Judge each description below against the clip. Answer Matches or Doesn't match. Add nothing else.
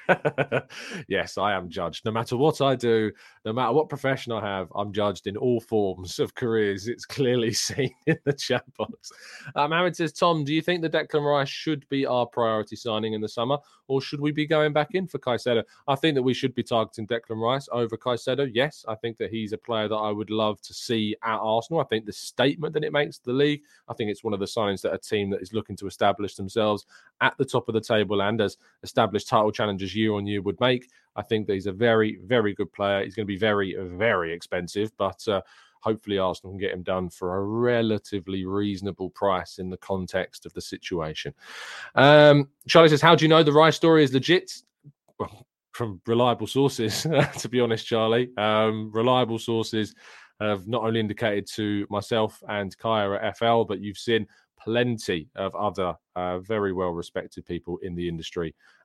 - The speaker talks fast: Matches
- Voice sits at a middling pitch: Doesn't match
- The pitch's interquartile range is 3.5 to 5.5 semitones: Matches